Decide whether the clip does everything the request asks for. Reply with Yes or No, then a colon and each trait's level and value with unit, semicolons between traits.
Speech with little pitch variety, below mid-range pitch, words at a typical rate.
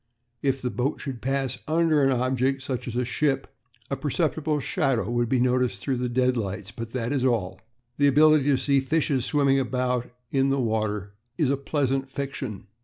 Yes: narrow, 2.2 semitones; low, 130 Hz; average, 180 wpm